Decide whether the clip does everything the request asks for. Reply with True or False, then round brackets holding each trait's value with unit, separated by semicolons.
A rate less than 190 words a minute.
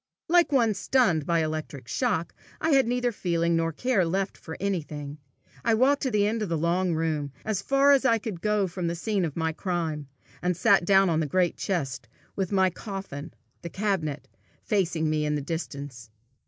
False (195 wpm)